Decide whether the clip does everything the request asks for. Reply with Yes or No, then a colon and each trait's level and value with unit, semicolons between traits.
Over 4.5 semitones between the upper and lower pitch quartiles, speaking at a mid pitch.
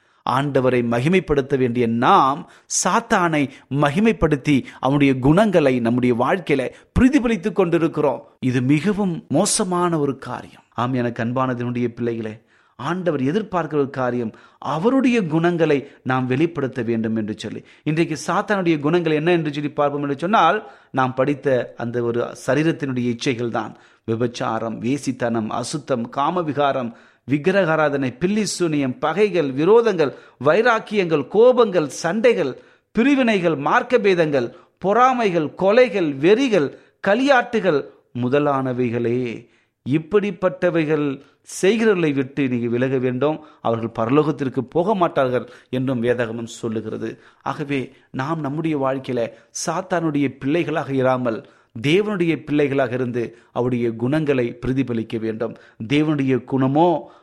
Yes: wide, 5.6 semitones; medium, 145 Hz